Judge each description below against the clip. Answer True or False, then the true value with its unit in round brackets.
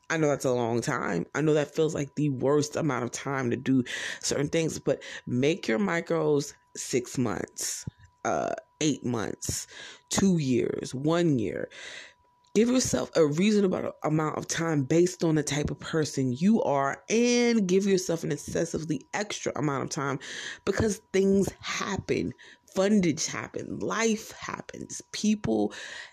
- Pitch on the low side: False (160 Hz)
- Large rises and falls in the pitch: True (6.7 semitones)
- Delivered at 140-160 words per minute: True (150 wpm)